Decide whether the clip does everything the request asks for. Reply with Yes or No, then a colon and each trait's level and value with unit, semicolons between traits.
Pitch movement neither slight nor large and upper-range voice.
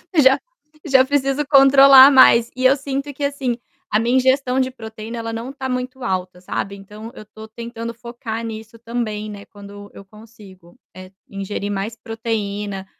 Yes: average, 3.9 semitones; high, 230 Hz